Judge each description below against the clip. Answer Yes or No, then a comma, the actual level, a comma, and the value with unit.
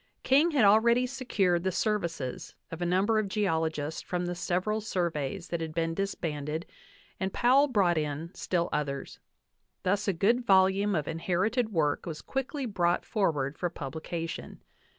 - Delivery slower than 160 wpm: Yes, average, 150 wpm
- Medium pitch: Yes, medium, 180 Hz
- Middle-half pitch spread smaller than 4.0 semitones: No, average, 4.5 semitones